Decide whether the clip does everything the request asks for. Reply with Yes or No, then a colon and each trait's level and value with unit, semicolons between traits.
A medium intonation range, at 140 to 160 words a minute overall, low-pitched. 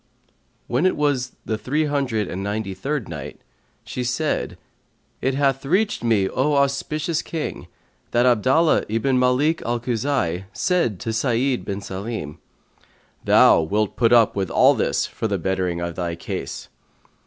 No: wide, 5.9 semitones; average, 150 wpm; low, 120 Hz